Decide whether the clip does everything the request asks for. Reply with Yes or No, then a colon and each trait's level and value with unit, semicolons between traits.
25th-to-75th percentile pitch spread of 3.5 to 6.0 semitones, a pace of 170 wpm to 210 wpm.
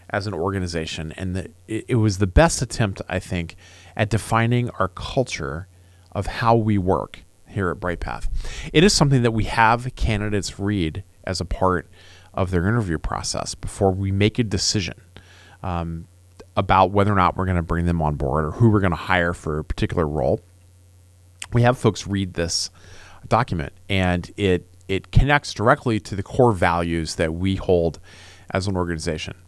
No: average, 3.1 semitones; average, 180 wpm